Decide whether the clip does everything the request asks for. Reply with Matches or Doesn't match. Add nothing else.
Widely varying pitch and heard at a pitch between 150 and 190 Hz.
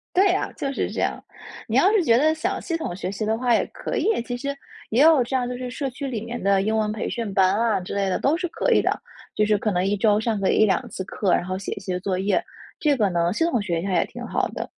Doesn't match